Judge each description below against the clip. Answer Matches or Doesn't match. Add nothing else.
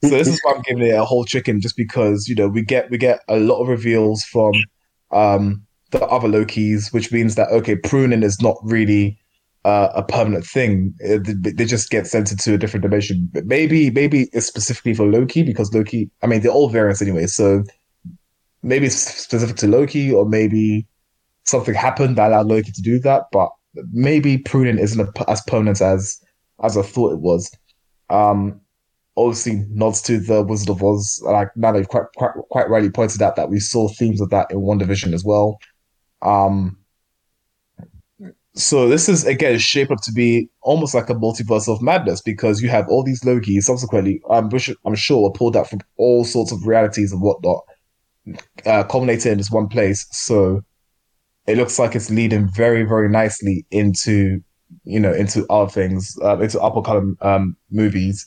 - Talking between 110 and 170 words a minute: Doesn't match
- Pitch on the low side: Matches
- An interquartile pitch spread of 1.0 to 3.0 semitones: Matches